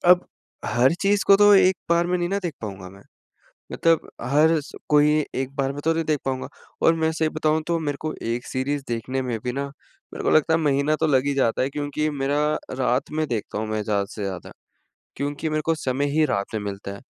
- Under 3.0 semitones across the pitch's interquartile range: No, average, 4.2 semitones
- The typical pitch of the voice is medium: Yes, medium, 145 Hz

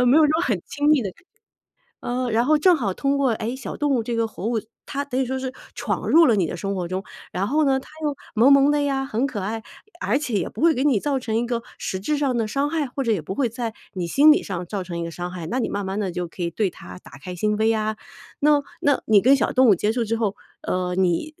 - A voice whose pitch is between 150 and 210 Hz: No, high, 230 Hz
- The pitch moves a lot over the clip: Yes, wide, 5.9 semitones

